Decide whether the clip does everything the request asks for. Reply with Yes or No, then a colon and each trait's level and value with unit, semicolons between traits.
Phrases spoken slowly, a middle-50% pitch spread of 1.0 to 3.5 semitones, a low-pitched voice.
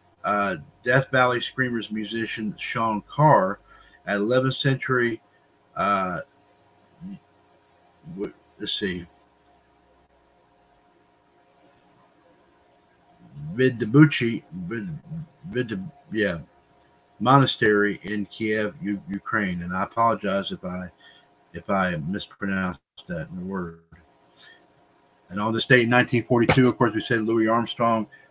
No: slow, 95 wpm; average, 4.5 semitones; low, 115 Hz